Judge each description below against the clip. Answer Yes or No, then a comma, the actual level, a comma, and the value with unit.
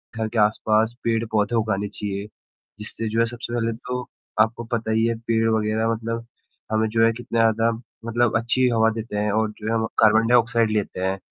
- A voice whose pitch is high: No, low, 115 Hz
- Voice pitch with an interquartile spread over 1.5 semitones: No, narrow, 1.1 semitones